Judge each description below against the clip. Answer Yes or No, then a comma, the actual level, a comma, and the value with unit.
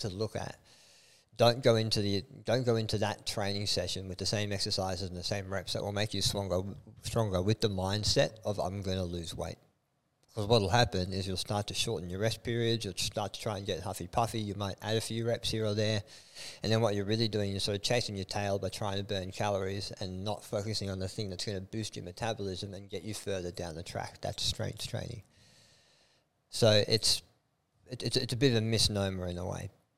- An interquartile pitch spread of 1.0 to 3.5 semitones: Yes, average, 2.9 semitones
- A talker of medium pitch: No, low, 105 Hz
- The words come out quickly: Yes, fast, 235 wpm